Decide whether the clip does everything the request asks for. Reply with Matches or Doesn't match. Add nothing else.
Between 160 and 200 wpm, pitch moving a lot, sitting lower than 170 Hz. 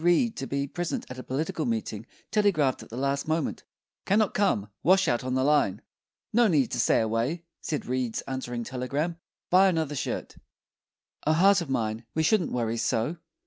Matches